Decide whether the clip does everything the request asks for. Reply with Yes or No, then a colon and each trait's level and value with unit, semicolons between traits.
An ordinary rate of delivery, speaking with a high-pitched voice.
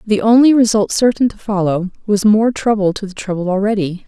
Yes: average, 190 wpm; high, 205 Hz